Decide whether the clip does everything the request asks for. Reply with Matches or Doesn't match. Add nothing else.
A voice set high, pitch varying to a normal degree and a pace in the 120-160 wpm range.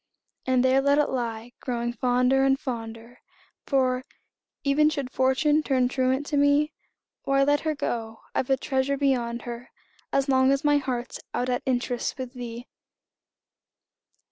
Doesn't match